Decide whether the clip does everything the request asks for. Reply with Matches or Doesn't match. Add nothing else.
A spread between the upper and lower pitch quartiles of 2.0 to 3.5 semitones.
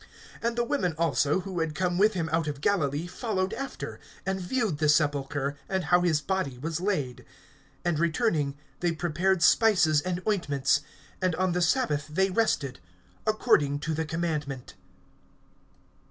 Doesn't match